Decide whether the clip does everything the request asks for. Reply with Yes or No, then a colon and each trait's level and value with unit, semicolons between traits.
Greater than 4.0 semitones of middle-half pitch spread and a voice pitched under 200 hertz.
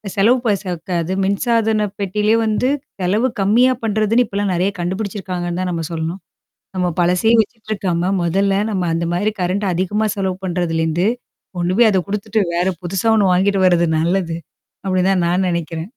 No: average, 3.2 semitones; high, 190 Hz